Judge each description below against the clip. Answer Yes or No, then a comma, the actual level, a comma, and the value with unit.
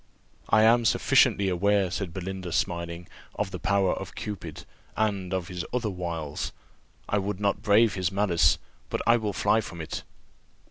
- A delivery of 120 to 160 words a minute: Yes, average, 155 wpm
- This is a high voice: No, very low, 95 Hz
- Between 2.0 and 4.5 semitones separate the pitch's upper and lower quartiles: Yes, average, 2.9 semitones